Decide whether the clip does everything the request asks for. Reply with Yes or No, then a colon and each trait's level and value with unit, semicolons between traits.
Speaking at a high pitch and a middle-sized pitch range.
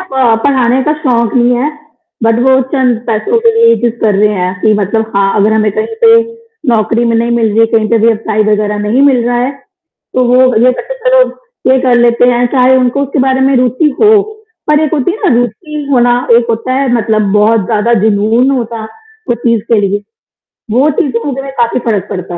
Yes: high, 240 Hz; average, 3.2 semitones